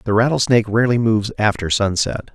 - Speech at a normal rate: Yes, average, 155 wpm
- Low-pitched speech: Yes, low, 110 Hz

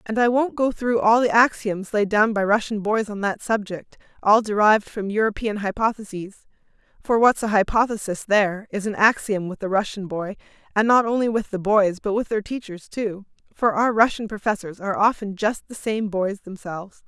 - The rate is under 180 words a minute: No, average, 195 wpm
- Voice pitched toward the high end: Yes, high, 210 Hz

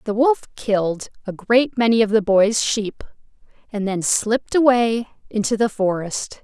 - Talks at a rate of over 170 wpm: No, average, 160 wpm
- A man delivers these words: No, female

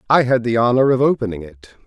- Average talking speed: No, fast, 225 wpm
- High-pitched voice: No, low, 115 Hz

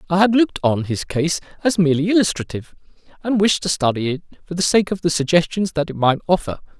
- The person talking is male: Yes, male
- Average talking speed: No, fast, 210 wpm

